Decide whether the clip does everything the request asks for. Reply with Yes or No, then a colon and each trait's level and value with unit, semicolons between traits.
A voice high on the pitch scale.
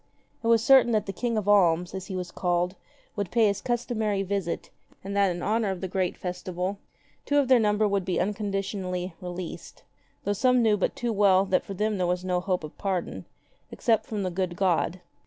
Yes: high, 195 Hz